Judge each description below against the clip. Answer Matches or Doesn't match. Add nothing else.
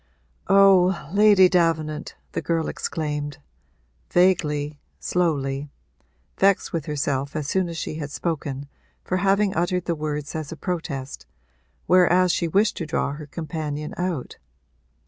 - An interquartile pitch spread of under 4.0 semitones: Matches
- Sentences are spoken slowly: Matches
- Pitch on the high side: Doesn't match